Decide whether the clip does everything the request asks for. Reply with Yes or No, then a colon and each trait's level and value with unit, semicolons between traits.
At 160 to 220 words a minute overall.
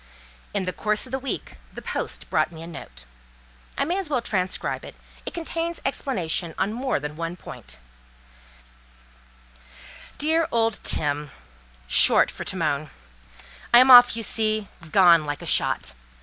No: average, 150 wpm